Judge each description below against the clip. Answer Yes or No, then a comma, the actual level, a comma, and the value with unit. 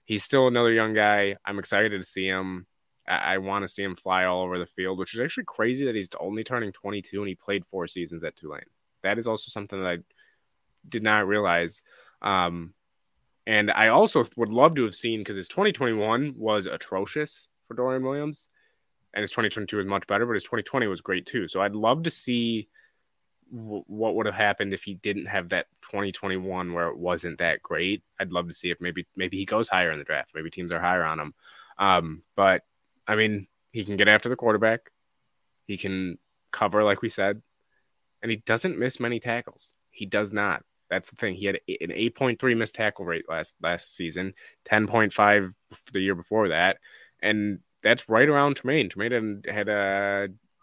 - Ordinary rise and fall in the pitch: Yes, average, 3.3 semitones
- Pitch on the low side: Yes, low, 105 Hz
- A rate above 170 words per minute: Yes, average, 195 wpm